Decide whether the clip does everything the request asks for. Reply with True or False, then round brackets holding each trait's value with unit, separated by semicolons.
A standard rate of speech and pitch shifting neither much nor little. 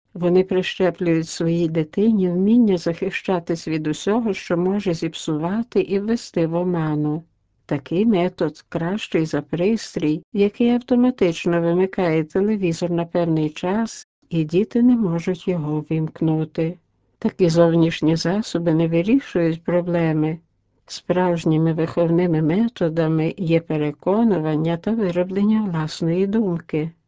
False (105 wpm; 3.0 semitones)